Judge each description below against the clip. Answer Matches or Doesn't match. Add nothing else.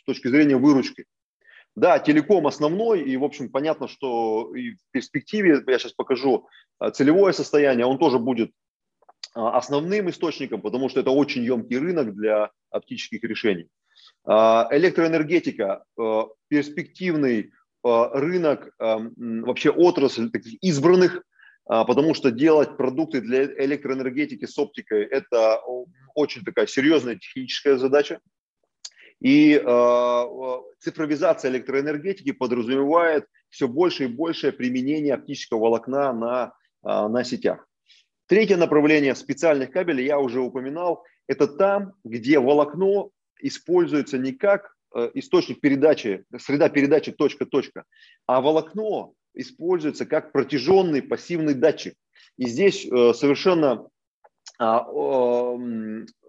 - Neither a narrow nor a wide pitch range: Doesn't match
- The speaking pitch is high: Doesn't match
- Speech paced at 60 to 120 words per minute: Matches